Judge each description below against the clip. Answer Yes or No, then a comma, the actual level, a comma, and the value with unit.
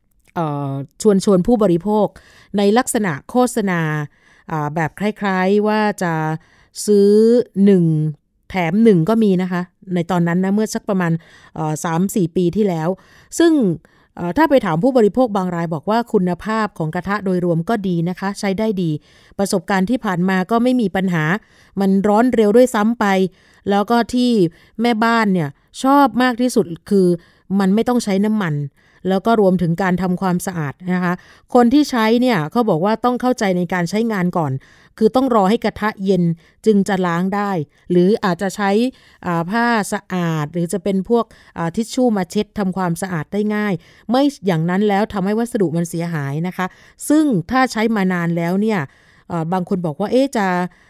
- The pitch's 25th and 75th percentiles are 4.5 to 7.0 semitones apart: No, average, 3.8 semitones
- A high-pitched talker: Yes, high, 195 Hz